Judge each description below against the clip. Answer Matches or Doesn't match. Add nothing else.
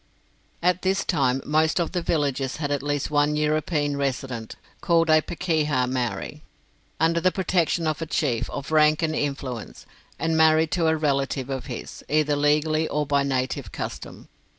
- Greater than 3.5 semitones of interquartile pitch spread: Doesn't match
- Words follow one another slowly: Doesn't match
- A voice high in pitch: Doesn't match